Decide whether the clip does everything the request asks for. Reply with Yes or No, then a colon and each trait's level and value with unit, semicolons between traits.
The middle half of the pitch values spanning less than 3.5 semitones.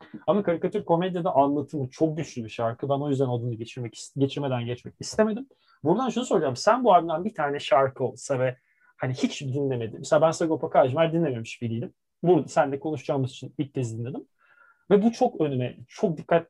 No: wide, 5.6 semitones